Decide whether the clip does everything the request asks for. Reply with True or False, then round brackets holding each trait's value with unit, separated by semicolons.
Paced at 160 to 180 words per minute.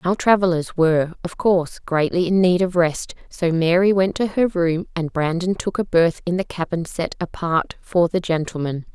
False (195 wpm)